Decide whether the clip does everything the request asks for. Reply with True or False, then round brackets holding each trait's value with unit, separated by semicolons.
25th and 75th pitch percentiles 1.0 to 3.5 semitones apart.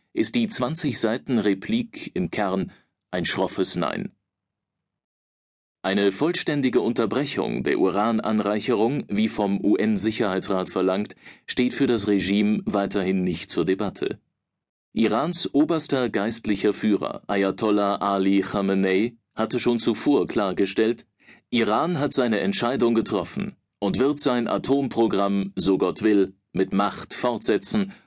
False (5.4 semitones)